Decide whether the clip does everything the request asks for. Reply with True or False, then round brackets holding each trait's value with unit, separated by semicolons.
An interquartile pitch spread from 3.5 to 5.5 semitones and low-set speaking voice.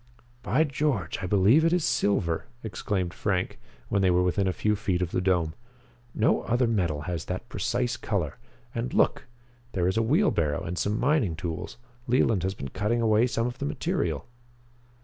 True (5.1 semitones; 100 Hz)